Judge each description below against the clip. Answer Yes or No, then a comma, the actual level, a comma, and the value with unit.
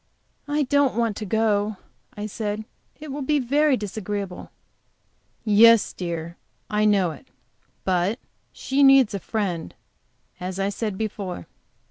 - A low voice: No, high, 210 Hz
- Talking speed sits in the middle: No, slow, 130 wpm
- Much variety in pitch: No, average, 3.6 semitones